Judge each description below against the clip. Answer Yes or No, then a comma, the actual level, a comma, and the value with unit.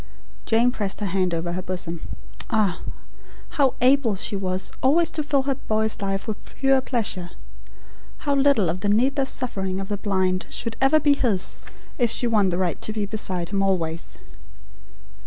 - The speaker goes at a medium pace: Yes, average, 175 wpm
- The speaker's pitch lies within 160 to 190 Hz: No, high, 210 Hz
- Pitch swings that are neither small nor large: No, wide, 5.8 semitones